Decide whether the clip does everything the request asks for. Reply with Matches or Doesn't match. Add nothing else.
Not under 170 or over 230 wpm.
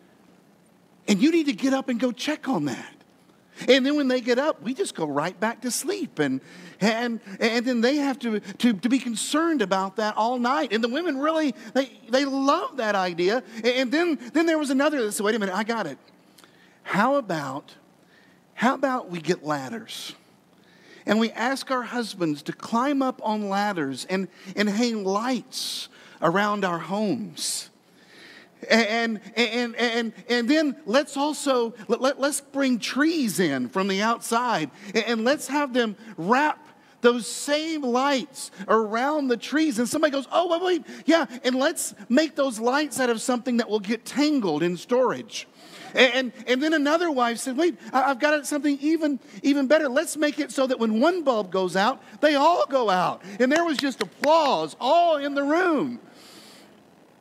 Matches